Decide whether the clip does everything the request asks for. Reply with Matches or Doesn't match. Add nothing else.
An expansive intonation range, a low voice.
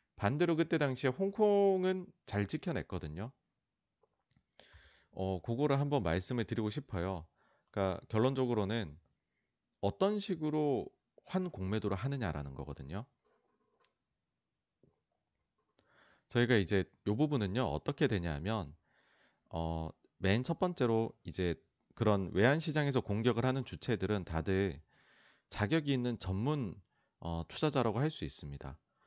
Matches